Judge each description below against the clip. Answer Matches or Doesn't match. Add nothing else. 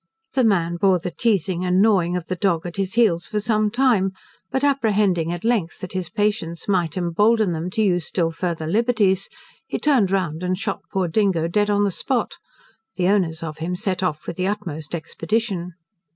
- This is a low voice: Doesn't match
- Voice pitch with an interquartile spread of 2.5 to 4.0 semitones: Matches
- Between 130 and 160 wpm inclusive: Doesn't match